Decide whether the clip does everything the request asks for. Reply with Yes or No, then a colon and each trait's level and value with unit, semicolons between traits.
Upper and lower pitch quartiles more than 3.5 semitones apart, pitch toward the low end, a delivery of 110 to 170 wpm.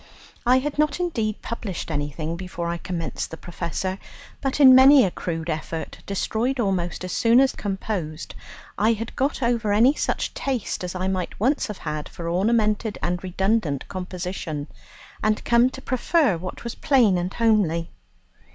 No: wide, 5.4 semitones; high, 200 Hz; average, 160 wpm